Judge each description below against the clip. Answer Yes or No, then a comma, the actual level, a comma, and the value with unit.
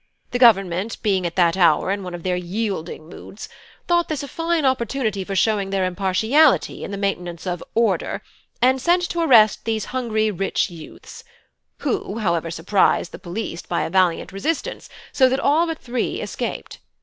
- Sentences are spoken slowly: No, average, 175 wpm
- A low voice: No, high, 205 Hz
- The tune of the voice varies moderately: No, wide, 6.2 semitones